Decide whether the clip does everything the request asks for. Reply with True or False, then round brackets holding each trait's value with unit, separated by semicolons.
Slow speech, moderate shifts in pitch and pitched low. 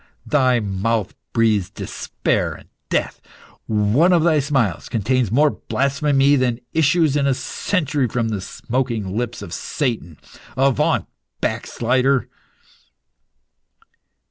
True (110 wpm; 4.0 semitones; 130 Hz)